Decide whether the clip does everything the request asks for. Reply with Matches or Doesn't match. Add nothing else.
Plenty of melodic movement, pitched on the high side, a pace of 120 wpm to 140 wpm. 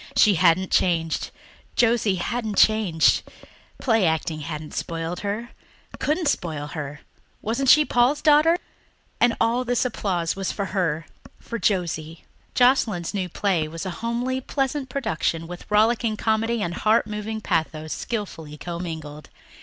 Matches